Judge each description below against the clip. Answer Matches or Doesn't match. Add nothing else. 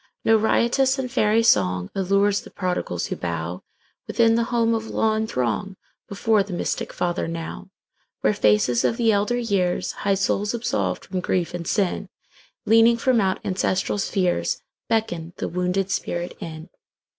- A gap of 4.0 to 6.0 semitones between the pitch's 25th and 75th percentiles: Matches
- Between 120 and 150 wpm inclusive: Matches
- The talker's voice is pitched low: Doesn't match